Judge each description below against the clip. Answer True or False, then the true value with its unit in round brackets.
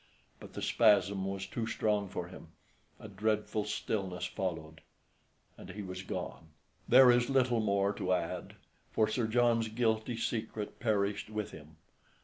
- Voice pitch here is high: False (105 Hz)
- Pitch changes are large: False (3.0 semitones)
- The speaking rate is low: False (145 wpm)